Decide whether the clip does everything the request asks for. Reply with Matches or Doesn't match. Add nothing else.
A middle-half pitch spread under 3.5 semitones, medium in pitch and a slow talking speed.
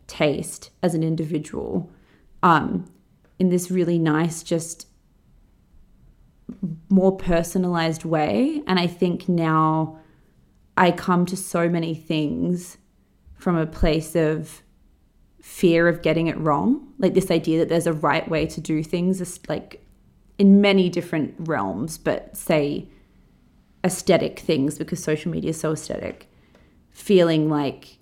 Matches